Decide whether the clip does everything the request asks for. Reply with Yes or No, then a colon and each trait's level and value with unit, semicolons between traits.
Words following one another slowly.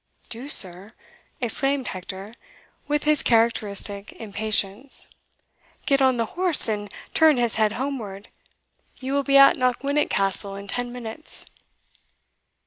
Yes: slow, 125 wpm